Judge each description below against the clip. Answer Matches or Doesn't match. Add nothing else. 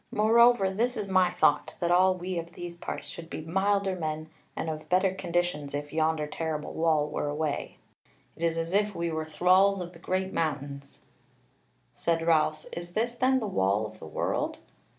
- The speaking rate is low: Doesn't match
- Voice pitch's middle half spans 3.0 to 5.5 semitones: Matches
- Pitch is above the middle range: Doesn't match